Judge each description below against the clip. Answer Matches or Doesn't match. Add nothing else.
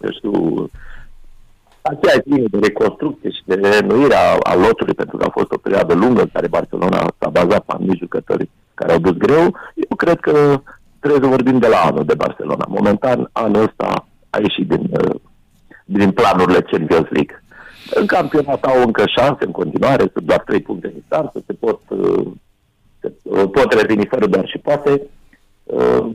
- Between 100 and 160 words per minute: Doesn't match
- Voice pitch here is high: Doesn't match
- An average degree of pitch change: Matches